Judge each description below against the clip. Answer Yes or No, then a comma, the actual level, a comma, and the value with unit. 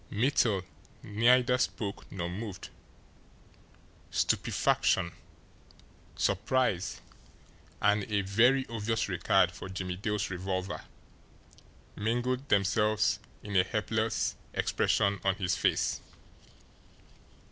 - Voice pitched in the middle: No, low, 105 Hz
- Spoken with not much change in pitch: No, average, 3.2 semitones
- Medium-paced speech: No, slow, 85 wpm